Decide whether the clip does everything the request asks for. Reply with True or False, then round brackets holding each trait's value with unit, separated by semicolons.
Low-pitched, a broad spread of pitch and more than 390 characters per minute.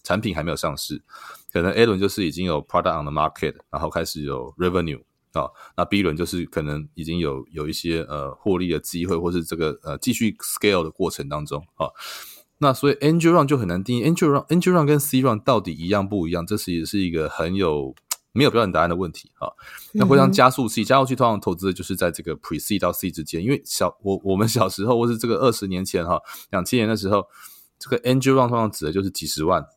True (95 Hz; 5.9 semitones; 440 characters per minute)